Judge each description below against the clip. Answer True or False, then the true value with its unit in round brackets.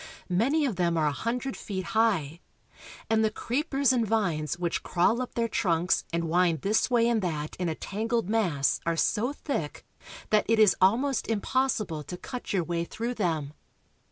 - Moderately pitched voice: False (205 Hz)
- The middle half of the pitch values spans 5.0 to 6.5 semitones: True (5.5 semitones)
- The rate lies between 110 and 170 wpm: False (180 wpm)